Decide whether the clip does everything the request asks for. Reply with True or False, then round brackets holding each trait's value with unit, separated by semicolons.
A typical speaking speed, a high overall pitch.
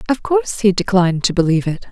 False (220 wpm; 195 Hz)